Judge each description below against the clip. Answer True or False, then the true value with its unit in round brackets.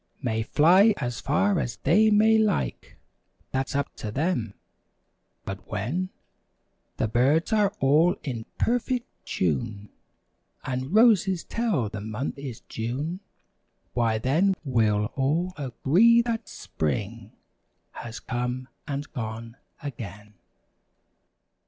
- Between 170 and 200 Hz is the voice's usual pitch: False (135 Hz)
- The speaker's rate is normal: False (110 wpm)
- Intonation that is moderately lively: False (8.6 semitones)